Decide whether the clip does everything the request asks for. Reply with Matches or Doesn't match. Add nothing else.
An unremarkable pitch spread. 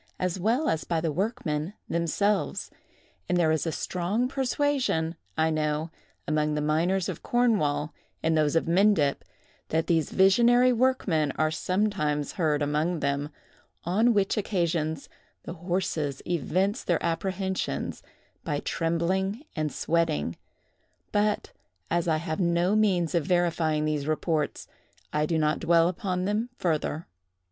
Matches